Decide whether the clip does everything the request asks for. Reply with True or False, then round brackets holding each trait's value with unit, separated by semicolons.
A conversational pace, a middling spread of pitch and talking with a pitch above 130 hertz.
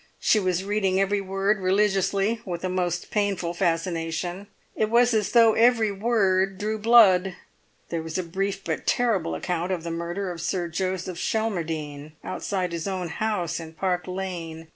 True (165 wpm; 3.1 semitones; 185 Hz)